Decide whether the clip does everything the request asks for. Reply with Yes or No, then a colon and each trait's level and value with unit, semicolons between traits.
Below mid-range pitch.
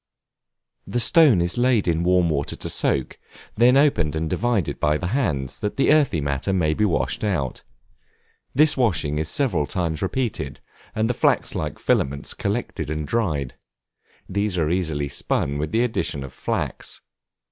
Yes: very low, 90 Hz